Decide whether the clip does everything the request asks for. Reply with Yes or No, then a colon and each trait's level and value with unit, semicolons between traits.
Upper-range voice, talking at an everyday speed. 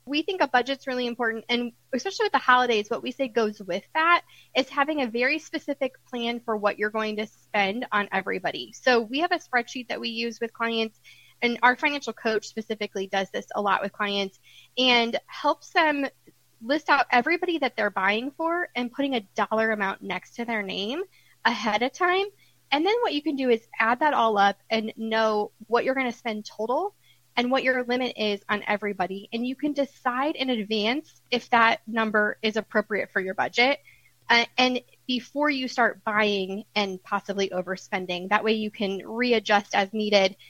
Yes: high, 235 Hz; average, 195 wpm